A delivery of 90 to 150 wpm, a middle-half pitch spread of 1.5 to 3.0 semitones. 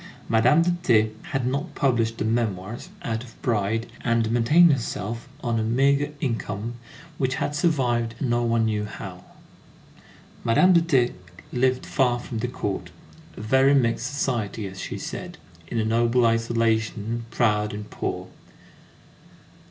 Yes: average, 145 wpm; average, 2.7 semitones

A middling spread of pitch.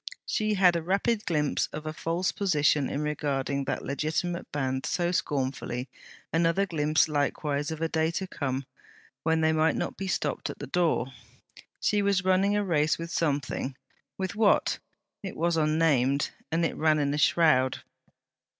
Yes: average, 3.5 semitones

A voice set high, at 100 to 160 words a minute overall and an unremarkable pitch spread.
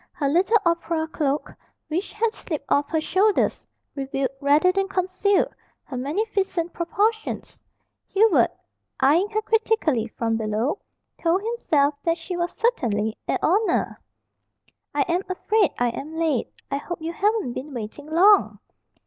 No: very high, 335 Hz; average, 140 wpm; wide, 6.0 semitones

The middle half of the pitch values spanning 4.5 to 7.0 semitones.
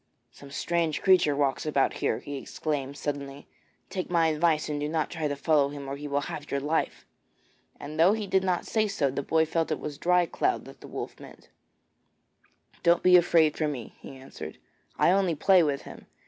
No: average, 3.4 semitones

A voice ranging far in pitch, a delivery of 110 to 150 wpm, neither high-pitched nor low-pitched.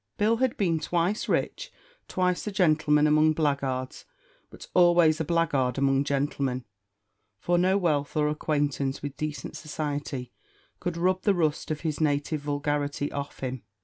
No: average, 3.3 semitones; average, 145 wpm; medium, 150 Hz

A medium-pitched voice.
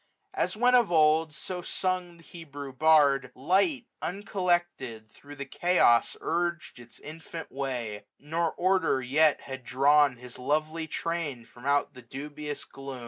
Yes: medium, 150 Hz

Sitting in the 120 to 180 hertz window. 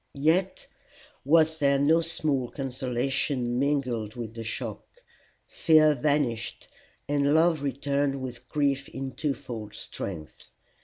Yes: medium, 140 Hz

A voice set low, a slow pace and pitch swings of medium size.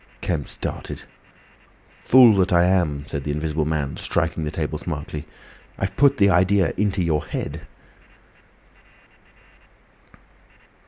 Yes: very low, 85 Hz; slow, 115 wpm; average, 3.9 semitones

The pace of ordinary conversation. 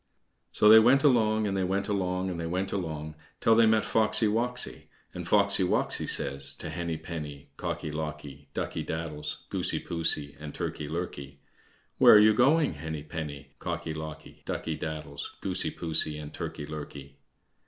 Yes: average, 165 wpm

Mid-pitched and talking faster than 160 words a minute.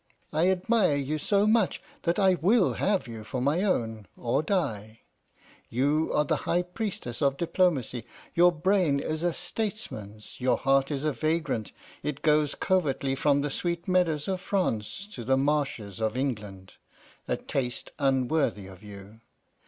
No: medium, 145 Hz; average, 155 wpm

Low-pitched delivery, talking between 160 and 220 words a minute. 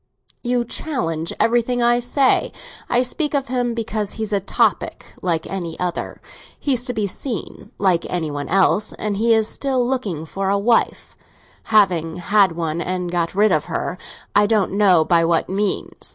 No: high, 205 Hz; average, 165 wpm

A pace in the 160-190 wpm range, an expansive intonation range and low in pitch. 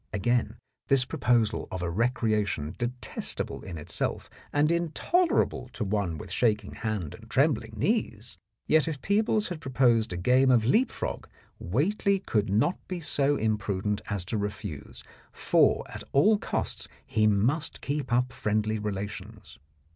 No: average, 145 wpm; wide, 5.7 semitones; low, 115 Hz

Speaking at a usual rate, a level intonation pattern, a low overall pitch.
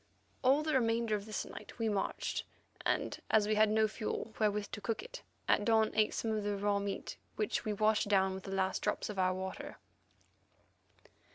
No: average, 195 wpm; narrow, 1.6 semitones; high, 215 Hz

